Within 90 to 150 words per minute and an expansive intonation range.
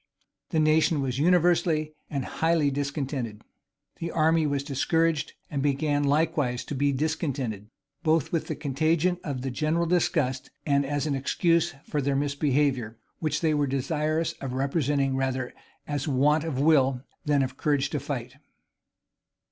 No: average, 145 wpm; average, 2.7 semitones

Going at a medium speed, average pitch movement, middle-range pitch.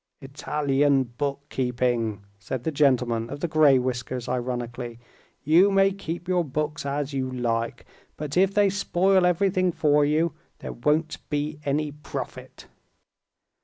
No: slow, 130 wpm; average, 4.2 semitones; medium, 145 Hz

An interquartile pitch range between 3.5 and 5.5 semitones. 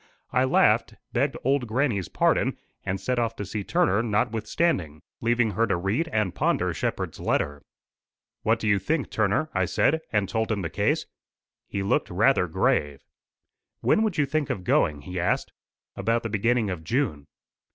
Yes: average, 4.4 semitones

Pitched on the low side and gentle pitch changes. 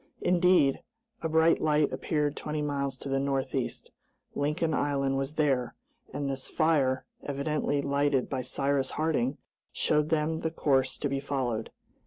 No: medium, 145 Hz; narrow, 2.1 semitones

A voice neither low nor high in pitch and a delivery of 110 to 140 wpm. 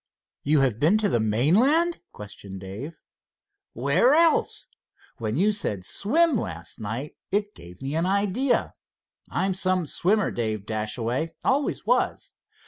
Yes: medium, 155 Hz; slow, 135 wpm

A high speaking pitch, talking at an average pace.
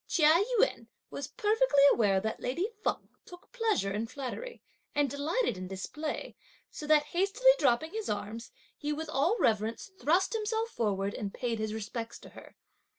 Yes: very high, 290 Hz; average, 160 wpm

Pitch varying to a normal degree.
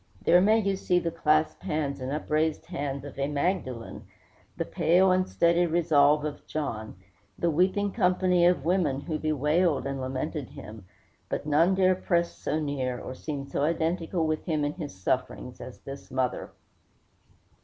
Yes: average, 4.0 semitones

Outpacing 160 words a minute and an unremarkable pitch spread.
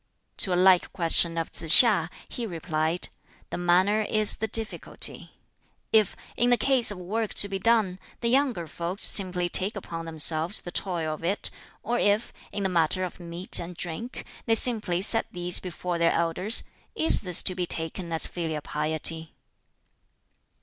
Yes: average, 170 wpm; average, 4.0 semitones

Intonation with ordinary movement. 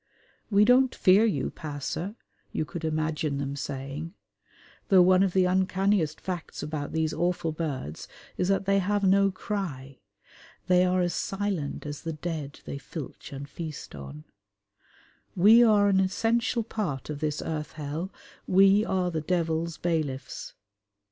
Yes: average, 4.5 semitones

